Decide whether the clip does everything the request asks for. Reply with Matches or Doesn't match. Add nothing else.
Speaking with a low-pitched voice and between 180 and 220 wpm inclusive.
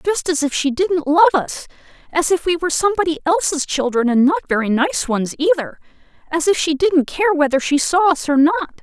Doesn't match